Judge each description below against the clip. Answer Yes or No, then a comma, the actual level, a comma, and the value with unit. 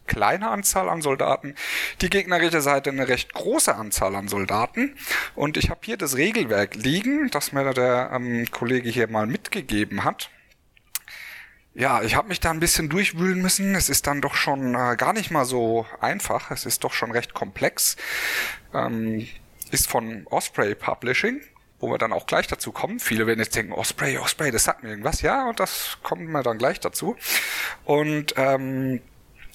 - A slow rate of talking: No, average, 180 wpm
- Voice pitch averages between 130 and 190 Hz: Yes, low, 135 Hz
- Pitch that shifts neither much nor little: No, wide, 6.7 semitones